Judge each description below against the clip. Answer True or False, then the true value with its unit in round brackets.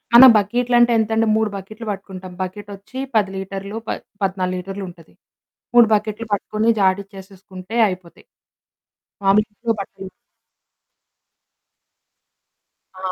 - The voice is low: False (200 Hz)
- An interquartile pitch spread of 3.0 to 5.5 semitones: False (2.5 semitones)